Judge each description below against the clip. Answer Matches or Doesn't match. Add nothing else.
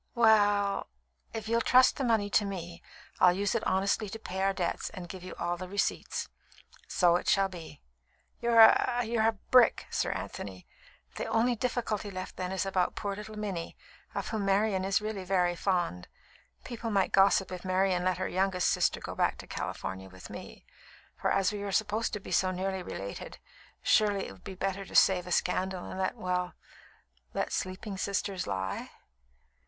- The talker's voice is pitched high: Matches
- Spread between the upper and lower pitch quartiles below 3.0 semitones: Matches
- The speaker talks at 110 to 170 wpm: Doesn't match